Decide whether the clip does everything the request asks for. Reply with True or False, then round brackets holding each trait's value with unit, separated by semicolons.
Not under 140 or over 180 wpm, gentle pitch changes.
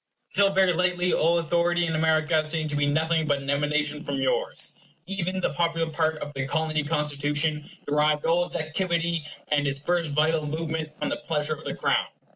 False (190 wpm; 2.2 semitones)